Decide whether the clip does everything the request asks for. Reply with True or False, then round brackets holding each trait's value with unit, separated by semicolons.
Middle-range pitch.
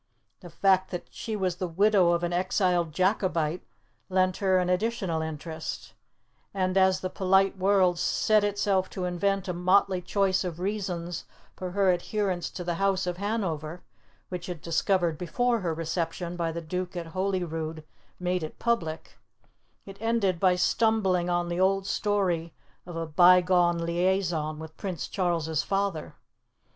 True (180 Hz)